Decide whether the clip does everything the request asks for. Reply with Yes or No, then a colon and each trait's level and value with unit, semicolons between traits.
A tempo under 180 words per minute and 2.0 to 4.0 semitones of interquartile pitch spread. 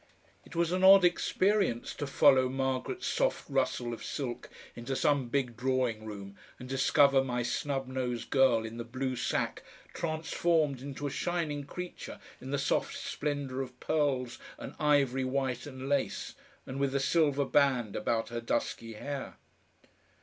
Yes: average, 155 wpm; narrow, 2.6 semitones